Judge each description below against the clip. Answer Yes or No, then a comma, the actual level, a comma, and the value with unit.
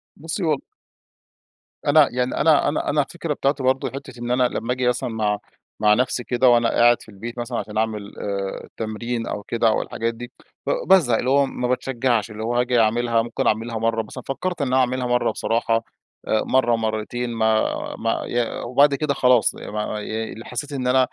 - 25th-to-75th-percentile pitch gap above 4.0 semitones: No, narrow, 2.6 semitones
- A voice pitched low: Yes, low, 120 Hz